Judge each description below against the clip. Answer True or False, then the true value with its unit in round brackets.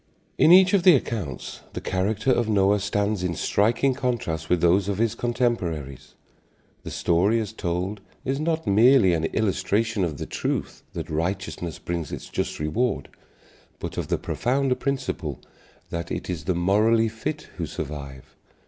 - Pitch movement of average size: False (5.7 semitones)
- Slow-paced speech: False (155 wpm)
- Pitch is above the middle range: False (100 Hz)